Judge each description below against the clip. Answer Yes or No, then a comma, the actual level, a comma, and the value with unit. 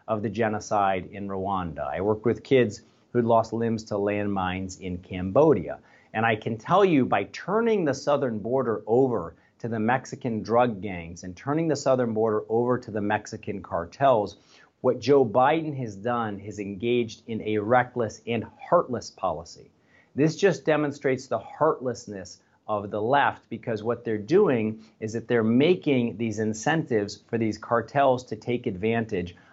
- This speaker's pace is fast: No, average, 160 wpm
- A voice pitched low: Yes, low, 115 Hz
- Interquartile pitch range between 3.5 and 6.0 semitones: No, average, 3.0 semitones